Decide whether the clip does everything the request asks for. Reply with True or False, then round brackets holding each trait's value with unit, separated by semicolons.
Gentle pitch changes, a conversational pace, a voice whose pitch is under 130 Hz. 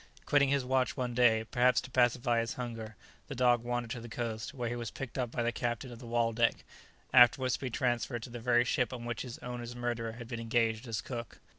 False (1.3 semitones; 235 wpm; 120 Hz)